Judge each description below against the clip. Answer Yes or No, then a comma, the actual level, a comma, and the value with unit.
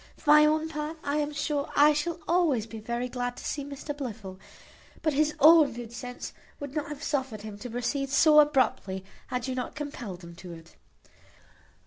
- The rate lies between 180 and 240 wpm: Yes, average, 190 wpm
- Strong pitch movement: No, average, 4.2 semitones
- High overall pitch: Yes, very high, 275 Hz